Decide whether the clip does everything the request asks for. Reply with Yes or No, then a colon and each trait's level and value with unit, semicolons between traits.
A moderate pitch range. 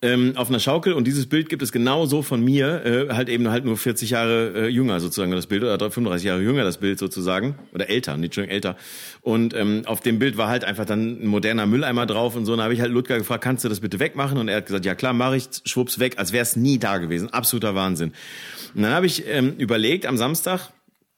Yes: average, 3.4 semitones